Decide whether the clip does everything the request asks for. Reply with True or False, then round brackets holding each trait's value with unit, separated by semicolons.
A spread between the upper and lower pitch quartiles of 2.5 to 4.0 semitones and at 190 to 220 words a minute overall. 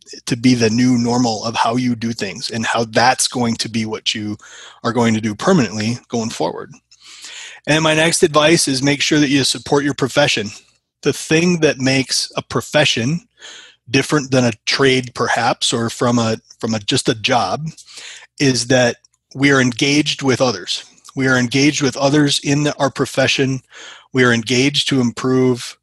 False (3.1 semitones; 180 wpm)